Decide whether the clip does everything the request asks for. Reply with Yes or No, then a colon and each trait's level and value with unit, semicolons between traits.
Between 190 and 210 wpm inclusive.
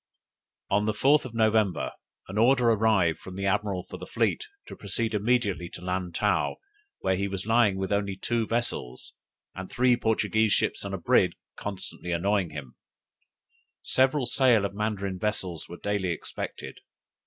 No: average, 155 wpm